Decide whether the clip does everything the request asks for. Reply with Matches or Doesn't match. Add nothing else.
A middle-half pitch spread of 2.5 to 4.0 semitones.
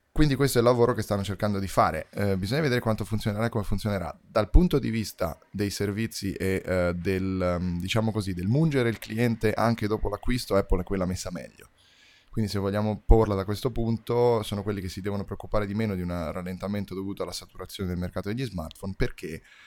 Matches